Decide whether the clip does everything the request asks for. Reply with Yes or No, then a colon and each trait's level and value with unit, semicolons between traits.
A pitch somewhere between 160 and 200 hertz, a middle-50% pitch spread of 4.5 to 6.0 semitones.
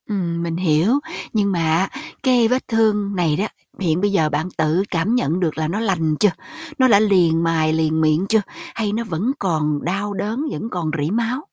Yes: medium, 185 Hz; average, 5.0 semitones